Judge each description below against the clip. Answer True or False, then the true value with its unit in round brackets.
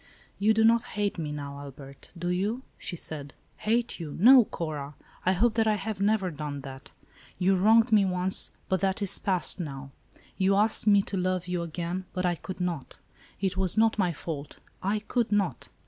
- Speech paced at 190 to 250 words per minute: True (195 wpm)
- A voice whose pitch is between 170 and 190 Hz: True (185 Hz)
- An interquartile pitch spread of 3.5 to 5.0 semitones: True (4.2 semitones)